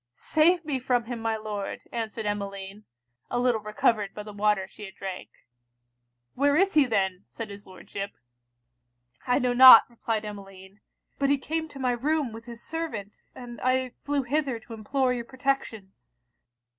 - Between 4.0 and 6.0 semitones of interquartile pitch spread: Yes, average, 4.3 semitones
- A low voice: No, high, 230 Hz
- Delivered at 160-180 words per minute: Yes, average, 165 wpm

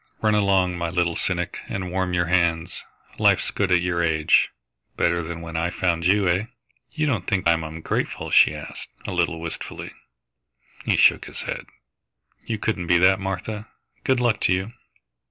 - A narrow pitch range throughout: Yes, narrow, 2.3 semitones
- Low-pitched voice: Yes, very low, 90 Hz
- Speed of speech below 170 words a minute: No, average, 175 wpm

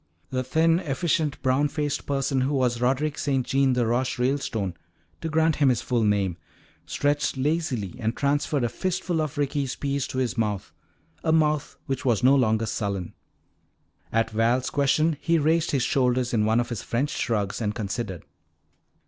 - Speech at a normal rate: Yes, average, 170 wpm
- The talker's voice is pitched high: No, low, 130 Hz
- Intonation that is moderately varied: Yes, average, 4.0 semitones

